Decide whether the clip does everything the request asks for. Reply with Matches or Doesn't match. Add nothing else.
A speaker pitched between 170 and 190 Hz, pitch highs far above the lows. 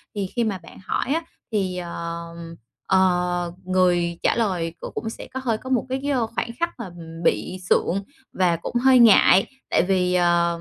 Doesn't match